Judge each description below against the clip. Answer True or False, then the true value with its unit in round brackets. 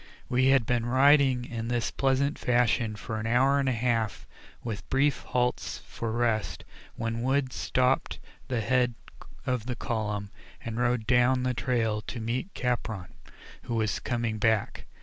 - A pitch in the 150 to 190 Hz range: False (120 Hz)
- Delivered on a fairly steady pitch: True (2.2 semitones)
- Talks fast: False (155 wpm)